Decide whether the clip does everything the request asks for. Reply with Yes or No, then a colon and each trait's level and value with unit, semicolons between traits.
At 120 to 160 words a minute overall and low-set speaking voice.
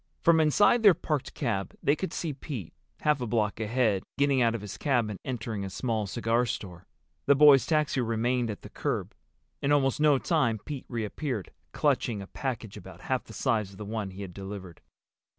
No: average, 195 wpm; low, 120 Hz